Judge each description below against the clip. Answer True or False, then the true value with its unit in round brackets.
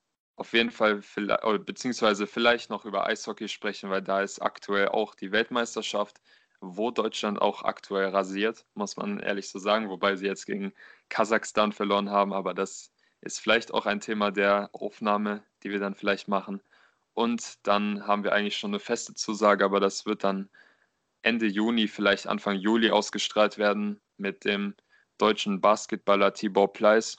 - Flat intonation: True (1.5 semitones)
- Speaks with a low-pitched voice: True (105 Hz)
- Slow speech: False (160 wpm)